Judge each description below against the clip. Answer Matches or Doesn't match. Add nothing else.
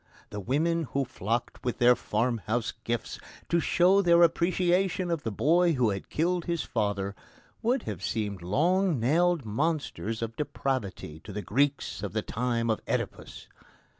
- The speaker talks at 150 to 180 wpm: Matches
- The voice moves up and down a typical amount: Doesn't match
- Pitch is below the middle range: Matches